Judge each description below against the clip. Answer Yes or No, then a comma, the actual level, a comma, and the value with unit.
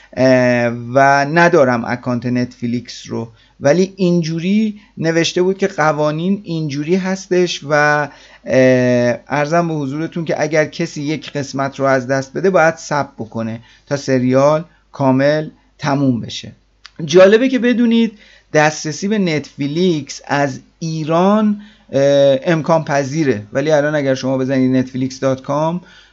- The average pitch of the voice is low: No, medium, 150 Hz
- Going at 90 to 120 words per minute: Yes, average, 115 wpm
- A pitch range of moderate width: Yes, average, 4.4 semitones